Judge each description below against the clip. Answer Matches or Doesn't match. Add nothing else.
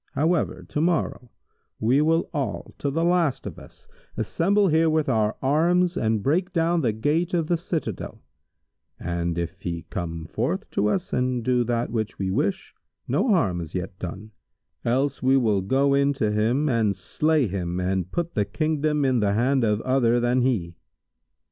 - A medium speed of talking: Matches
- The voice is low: Matches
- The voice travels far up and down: Matches